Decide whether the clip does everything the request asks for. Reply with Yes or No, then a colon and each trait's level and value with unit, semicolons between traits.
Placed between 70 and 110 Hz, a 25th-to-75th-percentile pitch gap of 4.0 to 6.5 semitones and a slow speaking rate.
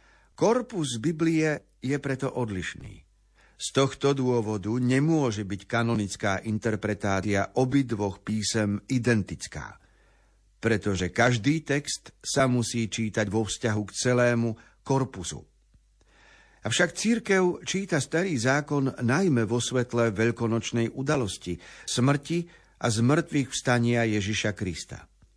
No: low, 120 Hz; average, 4.4 semitones; slow, 100 wpm